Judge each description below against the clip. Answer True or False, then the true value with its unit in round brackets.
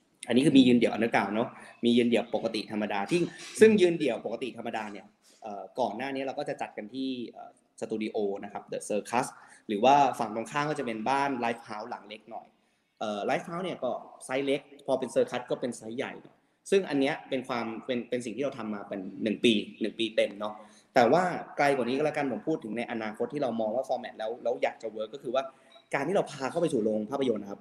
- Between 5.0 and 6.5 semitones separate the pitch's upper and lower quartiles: False (3.9 semitones)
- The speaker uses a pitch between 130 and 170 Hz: False (120 Hz)